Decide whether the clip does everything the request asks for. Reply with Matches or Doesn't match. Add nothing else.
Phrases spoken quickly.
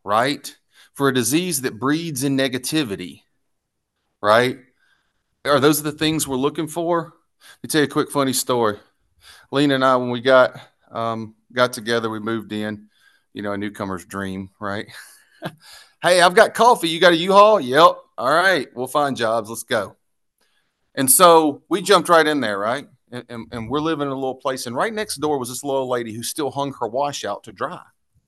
Doesn't match